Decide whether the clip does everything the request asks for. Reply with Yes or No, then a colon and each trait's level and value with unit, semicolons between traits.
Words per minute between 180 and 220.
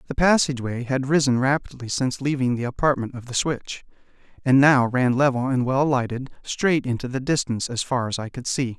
Yes: average, 200 wpm